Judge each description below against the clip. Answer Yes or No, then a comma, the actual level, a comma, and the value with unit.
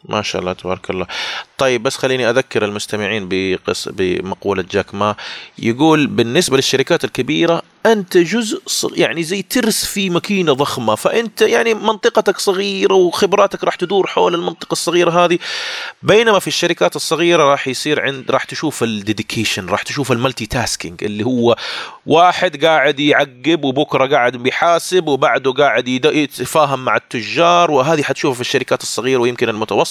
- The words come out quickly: Yes, fast, 145 wpm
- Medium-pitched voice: Yes, medium, 150 Hz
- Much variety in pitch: Yes, wide, 6.3 semitones